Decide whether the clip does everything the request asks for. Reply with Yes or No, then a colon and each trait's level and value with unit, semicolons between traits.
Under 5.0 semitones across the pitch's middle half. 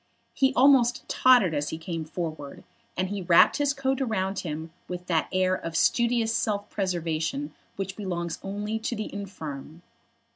No: wide, 5.4 semitones